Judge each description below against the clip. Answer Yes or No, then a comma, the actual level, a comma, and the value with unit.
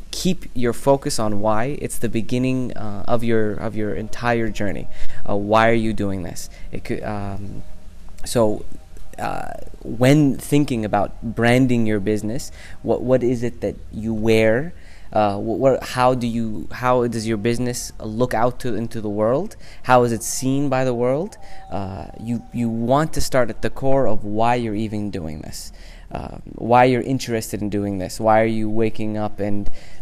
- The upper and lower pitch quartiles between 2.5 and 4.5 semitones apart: Yes, average, 3.1 semitones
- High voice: No, low, 110 Hz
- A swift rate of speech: No, average, 180 wpm